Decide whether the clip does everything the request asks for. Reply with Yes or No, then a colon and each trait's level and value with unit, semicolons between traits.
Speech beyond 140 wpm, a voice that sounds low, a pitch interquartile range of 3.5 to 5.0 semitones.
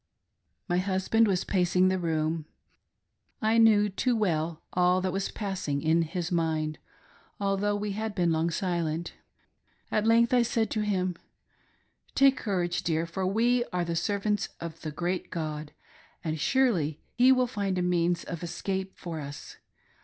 No: average, 160 wpm; medium, 185 Hz; average, 3.8 semitones